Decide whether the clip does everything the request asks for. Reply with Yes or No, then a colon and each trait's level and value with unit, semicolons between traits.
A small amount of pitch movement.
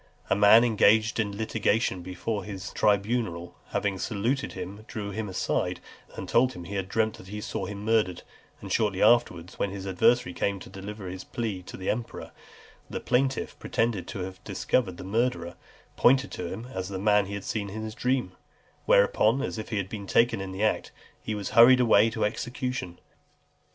No: average, 3.1 semitones